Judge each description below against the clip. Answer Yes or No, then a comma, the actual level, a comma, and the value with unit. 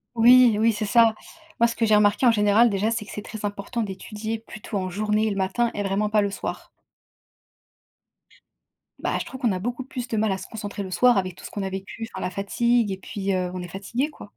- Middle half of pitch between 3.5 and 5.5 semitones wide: No, average, 2.8 semitones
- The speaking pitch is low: No, high, 210 Hz